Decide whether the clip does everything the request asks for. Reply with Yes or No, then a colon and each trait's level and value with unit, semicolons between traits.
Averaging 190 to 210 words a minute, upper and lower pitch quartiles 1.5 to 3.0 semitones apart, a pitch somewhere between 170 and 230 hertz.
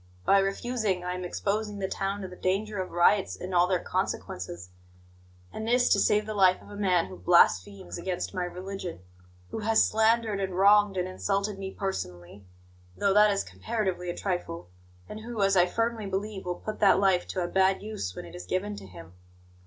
Yes: average, 200 wpm; average, 2.7 semitones; high, 190 Hz